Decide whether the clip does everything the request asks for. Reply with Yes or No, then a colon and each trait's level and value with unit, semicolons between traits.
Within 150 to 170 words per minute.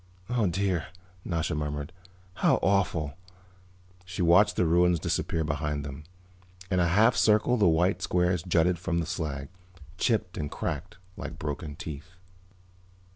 No: slow, 135 wpm